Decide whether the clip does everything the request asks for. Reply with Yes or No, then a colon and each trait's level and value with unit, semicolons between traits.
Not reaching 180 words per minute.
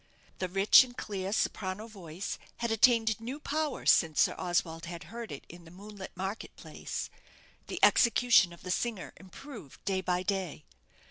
Yes: average, 160 wpm